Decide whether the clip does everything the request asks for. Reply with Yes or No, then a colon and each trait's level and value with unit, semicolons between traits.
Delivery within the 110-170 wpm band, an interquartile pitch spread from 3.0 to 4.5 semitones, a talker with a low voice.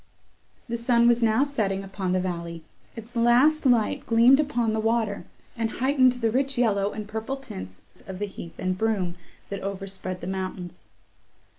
No: average, 165 wpm; average, 3.9 semitones; high, 220 Hz